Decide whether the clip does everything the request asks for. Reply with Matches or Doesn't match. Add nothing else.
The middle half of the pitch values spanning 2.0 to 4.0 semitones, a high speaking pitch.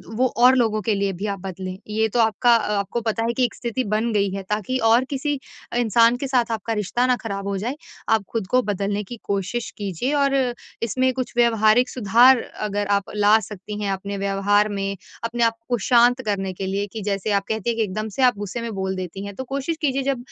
Matches